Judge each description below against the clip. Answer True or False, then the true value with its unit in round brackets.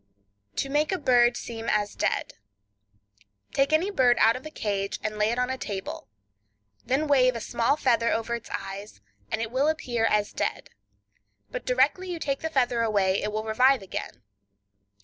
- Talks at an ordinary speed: True (175 wpm)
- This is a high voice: True (235 Hz)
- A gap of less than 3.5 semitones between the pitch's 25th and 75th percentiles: False (4.4 semitones)